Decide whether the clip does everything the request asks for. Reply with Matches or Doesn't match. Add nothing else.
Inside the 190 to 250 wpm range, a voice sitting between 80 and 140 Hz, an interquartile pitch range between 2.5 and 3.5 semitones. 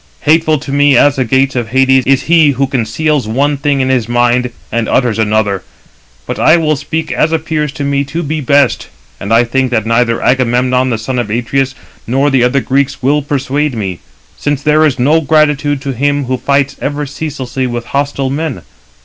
Matches